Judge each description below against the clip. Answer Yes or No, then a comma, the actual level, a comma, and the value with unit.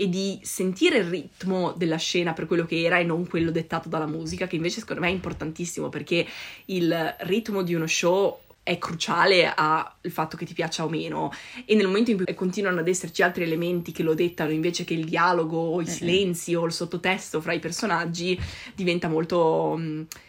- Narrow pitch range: Yes, narrow, 1.9 semitones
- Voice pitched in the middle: Yes, medium, 175 Hz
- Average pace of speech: No, fast, 200 wpm